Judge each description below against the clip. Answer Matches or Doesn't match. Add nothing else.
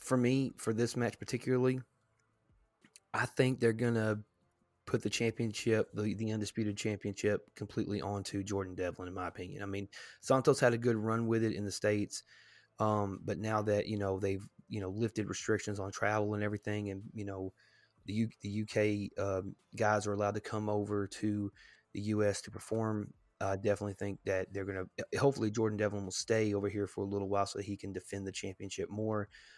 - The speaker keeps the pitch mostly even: Matches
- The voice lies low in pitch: Matches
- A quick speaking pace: Doesn't match